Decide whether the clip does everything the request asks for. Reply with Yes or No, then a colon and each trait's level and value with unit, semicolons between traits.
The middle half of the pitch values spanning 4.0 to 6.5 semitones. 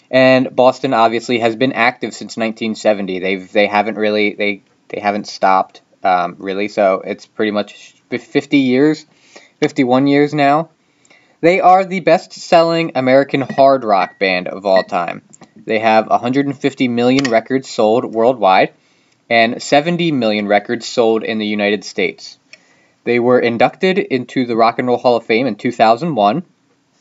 Yes: average, 4.3 semitones